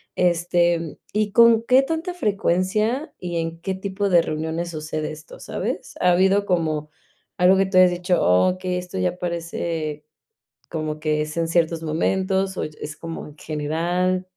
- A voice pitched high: No, medium, 175 Hz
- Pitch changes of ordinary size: Yes, average, 3.0 semitones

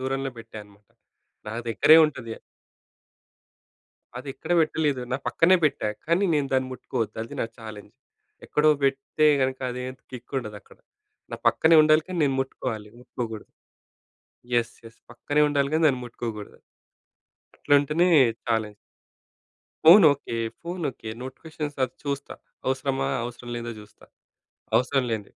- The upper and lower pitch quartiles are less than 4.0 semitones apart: No, average, 4.3 semitones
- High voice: No, low, 130 Hz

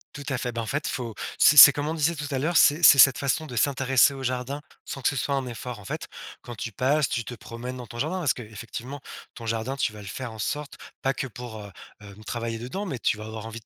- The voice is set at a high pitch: No, low, 125 Hz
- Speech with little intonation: No, average, 3.6 semitones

